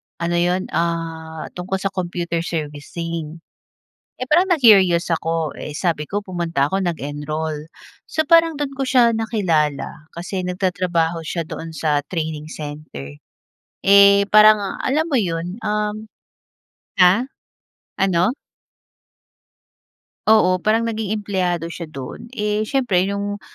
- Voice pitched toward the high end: No, medium, 180 Hz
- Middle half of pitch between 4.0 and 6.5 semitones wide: Yes, average, 4.5 semitones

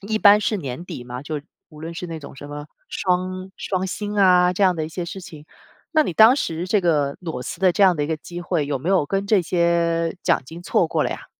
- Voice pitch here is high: No, medium, 175 Hz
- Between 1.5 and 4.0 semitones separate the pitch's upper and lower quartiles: Yes, average, 3.3 semitones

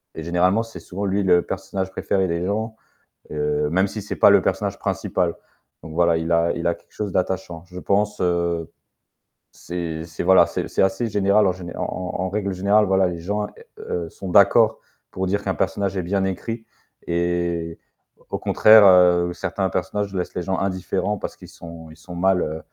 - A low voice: Yes, very low, 90 Hz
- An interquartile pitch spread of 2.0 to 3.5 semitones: Yes, narrow, 2.5 semitones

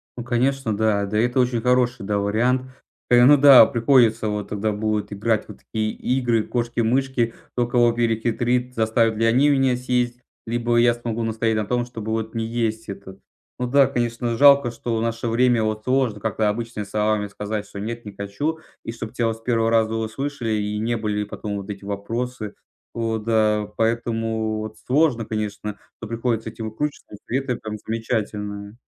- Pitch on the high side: No, low, 115 Hz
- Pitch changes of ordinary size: No, narrow, 2.2 semitones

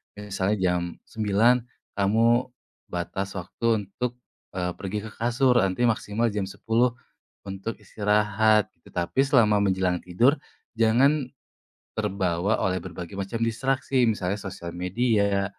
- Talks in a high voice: No, low, 105 Hz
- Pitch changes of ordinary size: Yes, average, 3.5 semitones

